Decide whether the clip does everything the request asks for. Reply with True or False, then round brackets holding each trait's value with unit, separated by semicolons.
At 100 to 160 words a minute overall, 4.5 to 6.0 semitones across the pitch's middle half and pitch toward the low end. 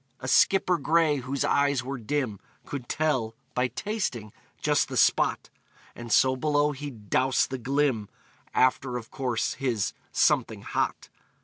False (140 wpm; 3.3 semitones; 130 Hz)